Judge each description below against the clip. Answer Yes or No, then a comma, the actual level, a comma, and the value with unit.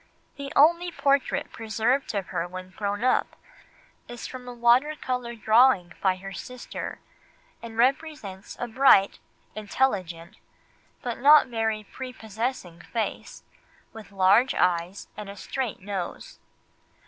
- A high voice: Yes, high, 225 Hz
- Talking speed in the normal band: No, slow, 125 wpm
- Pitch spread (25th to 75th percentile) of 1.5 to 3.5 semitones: No, average, 4.7 semitones